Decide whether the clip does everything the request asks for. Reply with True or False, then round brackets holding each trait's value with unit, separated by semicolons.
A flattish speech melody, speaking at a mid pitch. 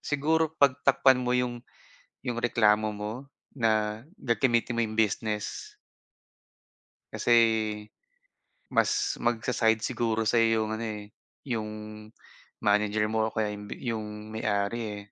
False (2.2 semitones; 110 Hz)